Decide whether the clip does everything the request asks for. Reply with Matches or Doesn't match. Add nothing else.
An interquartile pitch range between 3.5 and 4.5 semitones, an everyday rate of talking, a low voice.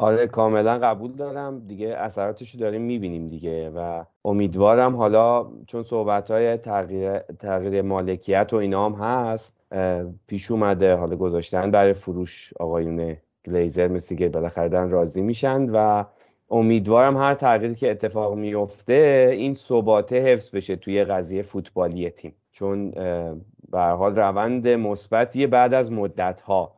Matches